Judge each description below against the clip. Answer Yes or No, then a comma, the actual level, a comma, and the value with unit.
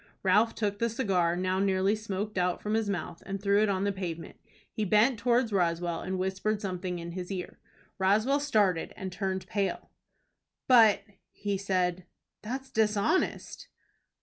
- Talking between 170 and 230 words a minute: No, average, 155 wpm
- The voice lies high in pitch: Yes, high, 195 Hz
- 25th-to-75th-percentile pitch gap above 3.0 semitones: No, narrow, 2.6 semitones